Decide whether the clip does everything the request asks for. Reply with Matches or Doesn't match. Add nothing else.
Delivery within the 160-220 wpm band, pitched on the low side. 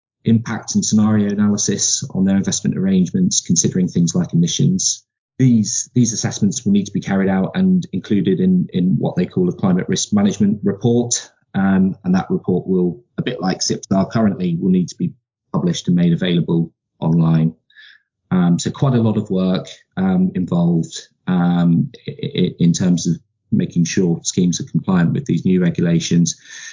Doesn't match